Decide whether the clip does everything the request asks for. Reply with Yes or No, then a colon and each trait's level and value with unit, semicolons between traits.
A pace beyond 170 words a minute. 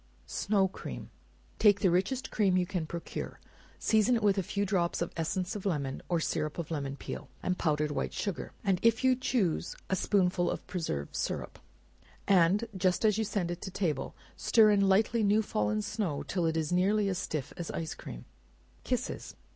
Yes: average, 185 wpm